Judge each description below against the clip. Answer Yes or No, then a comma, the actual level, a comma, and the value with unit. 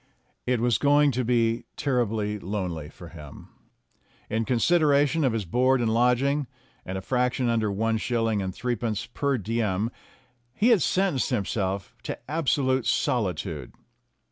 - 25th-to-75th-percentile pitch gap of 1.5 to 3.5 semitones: No, average, 3.9 semitones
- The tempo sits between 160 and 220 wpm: No, average, 145 wpm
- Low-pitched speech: Yes, low, 120 Hz